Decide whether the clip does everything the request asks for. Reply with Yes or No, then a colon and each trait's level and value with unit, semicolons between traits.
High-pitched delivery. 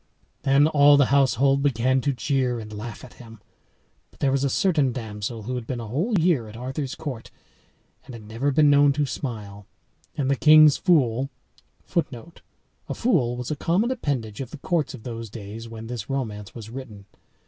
No: low, 130 Hz